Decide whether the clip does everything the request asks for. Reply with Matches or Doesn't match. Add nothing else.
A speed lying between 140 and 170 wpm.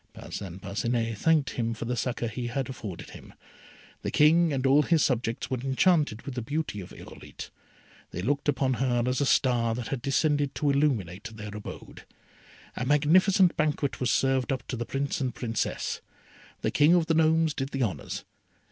Doesn't match